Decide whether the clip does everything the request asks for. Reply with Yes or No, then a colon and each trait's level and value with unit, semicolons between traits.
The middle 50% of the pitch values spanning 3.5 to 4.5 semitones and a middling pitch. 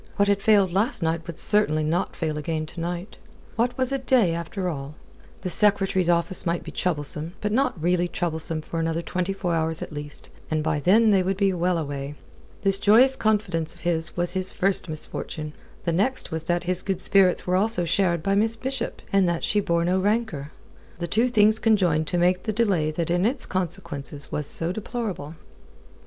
Yes: average, 3.8 semitones; medium, 180 Hz